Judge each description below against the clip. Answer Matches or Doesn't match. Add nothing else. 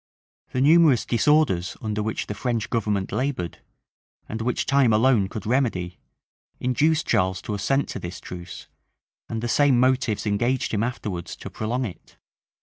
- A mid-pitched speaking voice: Doesn't match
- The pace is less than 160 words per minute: Matches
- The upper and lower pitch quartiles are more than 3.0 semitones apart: Matches